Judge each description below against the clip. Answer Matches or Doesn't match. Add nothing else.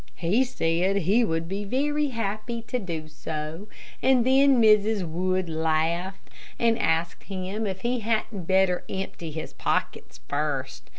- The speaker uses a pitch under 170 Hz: Doesn't match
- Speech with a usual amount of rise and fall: Doesn't match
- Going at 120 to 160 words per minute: Matches